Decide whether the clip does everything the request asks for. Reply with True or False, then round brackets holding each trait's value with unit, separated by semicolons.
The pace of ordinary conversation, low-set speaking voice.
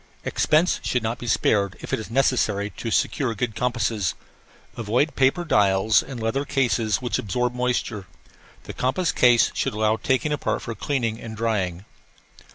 True (160 wpm; 115 Hz)